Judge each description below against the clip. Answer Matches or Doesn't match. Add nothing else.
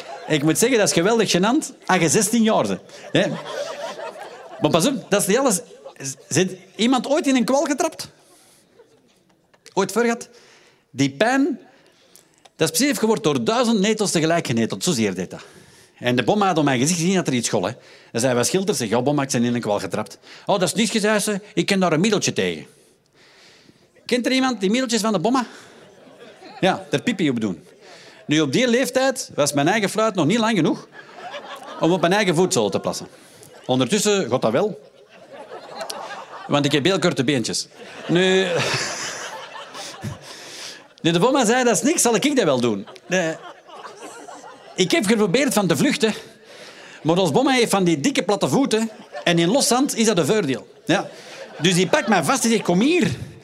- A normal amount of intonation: Doesn't match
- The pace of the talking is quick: Doesn't match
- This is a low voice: Doesn't match